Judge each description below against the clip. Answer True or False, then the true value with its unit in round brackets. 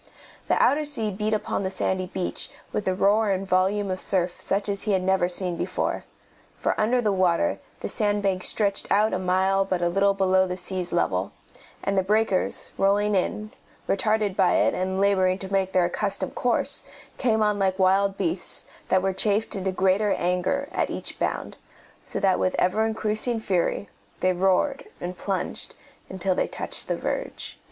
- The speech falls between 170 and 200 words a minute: True (180 wpm)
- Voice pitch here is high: True (195 Hz)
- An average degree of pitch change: False (2.1 semitones)